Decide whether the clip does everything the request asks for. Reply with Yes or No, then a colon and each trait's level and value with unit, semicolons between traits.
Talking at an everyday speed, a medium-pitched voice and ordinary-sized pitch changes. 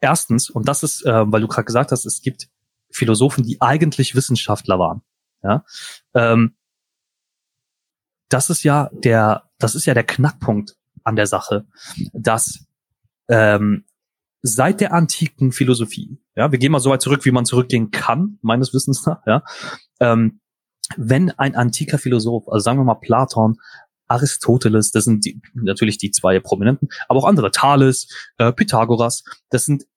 No: average, 155 wpm; low, 125 Hz; average, 3.5 semitones